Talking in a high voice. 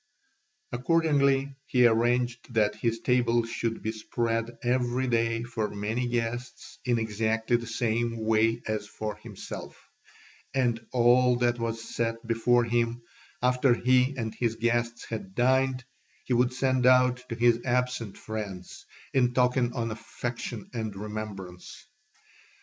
No: low, 120 Hz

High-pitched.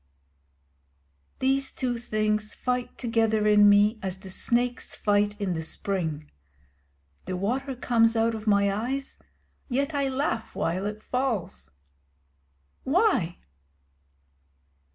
Yes: high, 220 Hz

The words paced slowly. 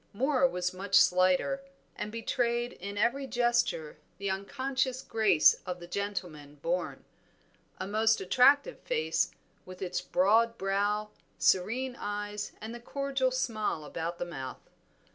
Yes: slow, 130 wpm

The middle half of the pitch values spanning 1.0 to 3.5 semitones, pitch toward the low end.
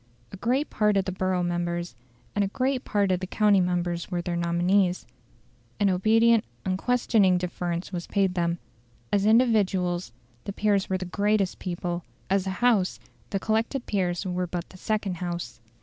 No: average, 2.9 semitones; medium, 185 Hz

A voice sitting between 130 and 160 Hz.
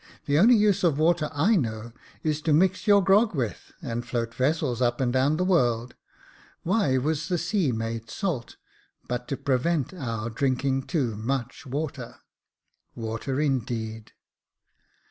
Yes: low, 135 Hz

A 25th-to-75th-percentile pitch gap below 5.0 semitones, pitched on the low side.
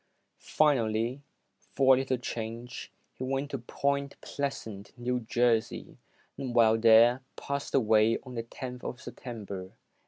Yes: average, 2.9 semitones; low, 120 Hz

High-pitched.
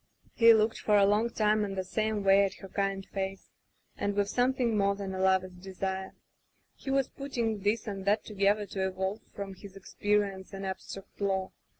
Yes: high, 200 Hz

